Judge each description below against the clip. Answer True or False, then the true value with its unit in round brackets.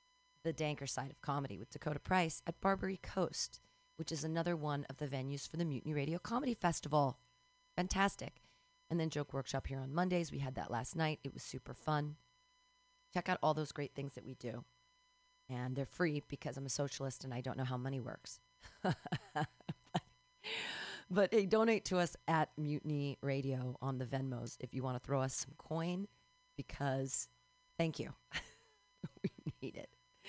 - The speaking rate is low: False (175 wpm)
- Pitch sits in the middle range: True (145 Hz)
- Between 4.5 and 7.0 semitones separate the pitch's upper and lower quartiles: True (5.1 semitones)